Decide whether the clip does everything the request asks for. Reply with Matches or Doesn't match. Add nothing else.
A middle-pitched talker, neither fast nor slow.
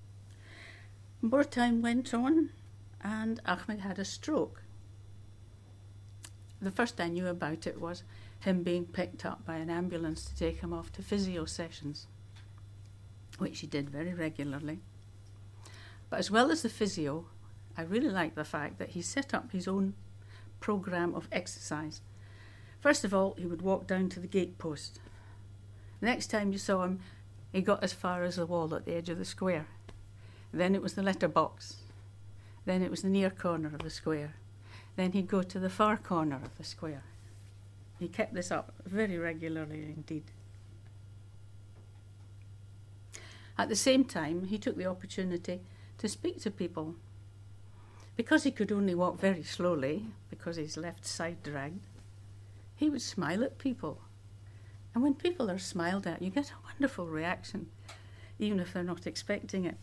Matches